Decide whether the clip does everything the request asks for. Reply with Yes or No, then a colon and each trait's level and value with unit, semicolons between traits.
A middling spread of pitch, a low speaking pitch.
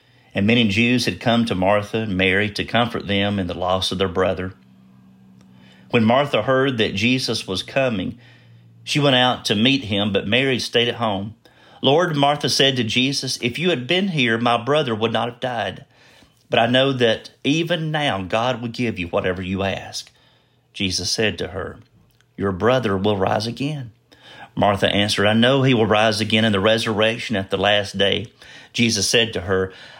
Yes: average, 4.3 semitones; low, 110 Hz